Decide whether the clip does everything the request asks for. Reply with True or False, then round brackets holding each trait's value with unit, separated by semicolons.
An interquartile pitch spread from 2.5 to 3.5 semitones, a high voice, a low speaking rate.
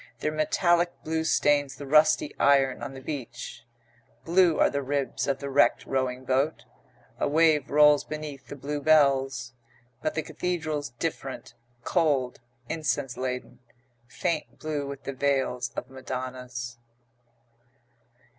False (2.8 semitones; 140 Hz; 130 wpm)